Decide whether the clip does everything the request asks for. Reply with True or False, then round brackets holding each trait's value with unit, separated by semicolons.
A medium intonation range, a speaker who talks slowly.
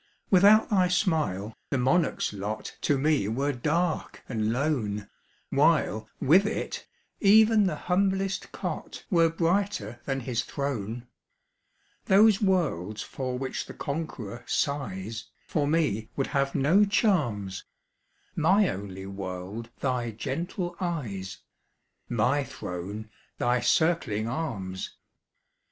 False (8.2 semitones; 110 wpm)